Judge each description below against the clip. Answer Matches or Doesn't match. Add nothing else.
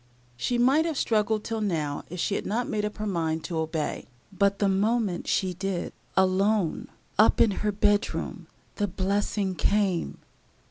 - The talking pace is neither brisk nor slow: Matches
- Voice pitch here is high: Matches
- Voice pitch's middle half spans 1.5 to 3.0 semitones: Matches